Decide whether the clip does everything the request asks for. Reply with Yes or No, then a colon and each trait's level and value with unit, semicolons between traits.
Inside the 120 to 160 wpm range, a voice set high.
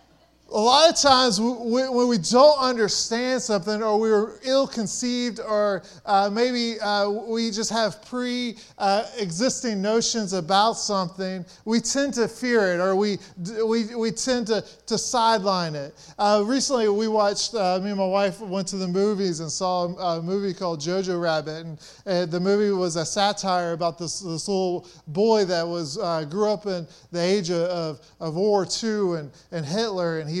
No: average, 175 wpm; high, 200 Hz